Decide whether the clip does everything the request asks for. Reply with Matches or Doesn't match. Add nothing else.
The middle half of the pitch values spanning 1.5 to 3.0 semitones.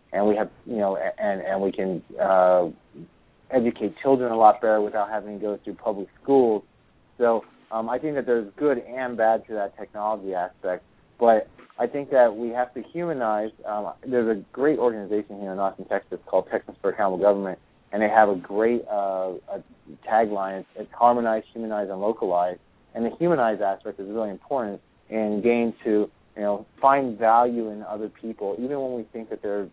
Matches